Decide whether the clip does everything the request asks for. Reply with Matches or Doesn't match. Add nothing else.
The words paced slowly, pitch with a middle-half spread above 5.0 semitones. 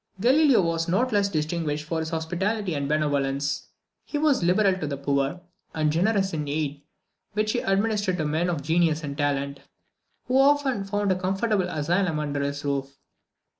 Doesn't match